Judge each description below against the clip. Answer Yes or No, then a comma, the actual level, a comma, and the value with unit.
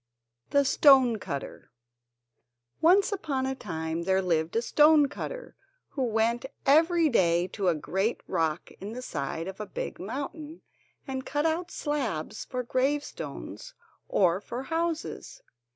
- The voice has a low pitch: No, very high, 255 Hz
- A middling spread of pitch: No, wide, 8.0 semitones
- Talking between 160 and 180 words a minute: No, average, 140 wpm